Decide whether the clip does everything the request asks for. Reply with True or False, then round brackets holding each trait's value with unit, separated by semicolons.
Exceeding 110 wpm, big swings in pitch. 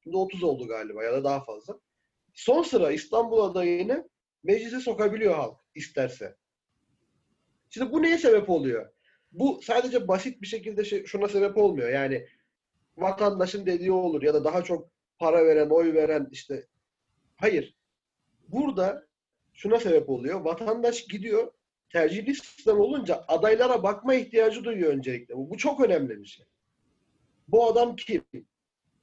True (135 wpm; 6.7 semitones)